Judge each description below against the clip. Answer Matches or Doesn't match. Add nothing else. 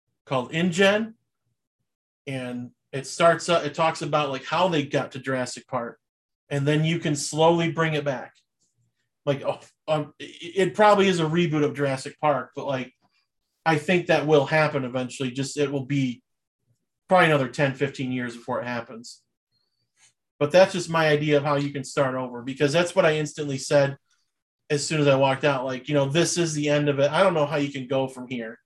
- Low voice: Doesn't match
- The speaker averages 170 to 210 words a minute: Matches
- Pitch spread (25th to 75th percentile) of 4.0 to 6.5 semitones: Doesn't match